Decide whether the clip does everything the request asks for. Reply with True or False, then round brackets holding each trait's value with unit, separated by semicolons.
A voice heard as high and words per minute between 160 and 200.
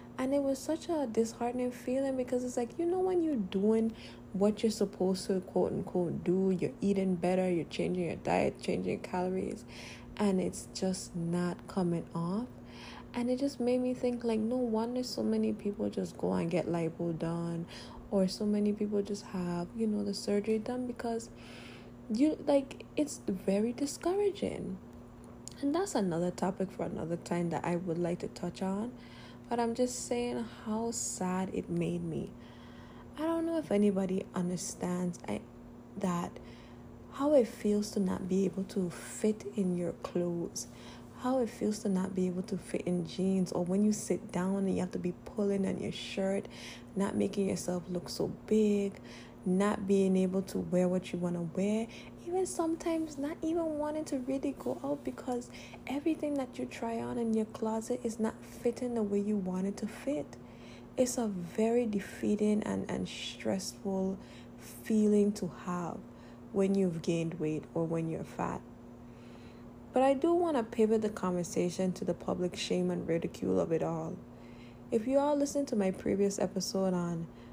True (195 Hz; 175 wpm)